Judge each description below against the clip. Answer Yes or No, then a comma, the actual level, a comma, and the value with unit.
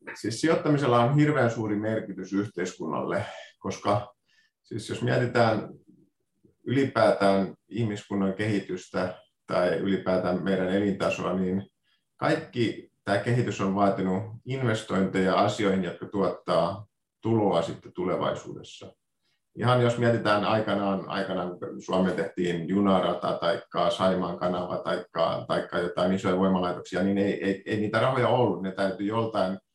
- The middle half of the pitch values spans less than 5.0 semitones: Yes, average, 2.7 semitones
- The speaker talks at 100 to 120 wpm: Yes, average, 115 wpm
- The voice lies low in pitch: Yes, low, 100 Hz